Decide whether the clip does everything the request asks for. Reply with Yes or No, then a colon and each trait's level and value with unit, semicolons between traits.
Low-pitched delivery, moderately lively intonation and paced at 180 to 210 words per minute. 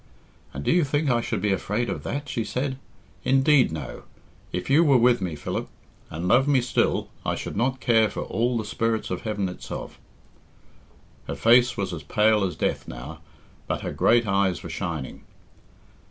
No: low, 115 Hz; wide, 5.8 semitones; average, 185 wpm